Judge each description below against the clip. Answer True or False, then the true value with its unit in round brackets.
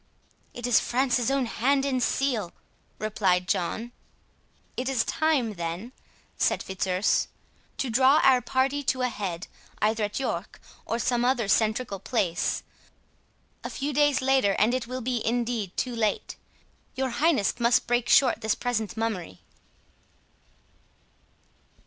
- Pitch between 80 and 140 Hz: False (240 Hz)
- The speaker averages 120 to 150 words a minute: True (135 wpm)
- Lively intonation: False (3.6 semitones)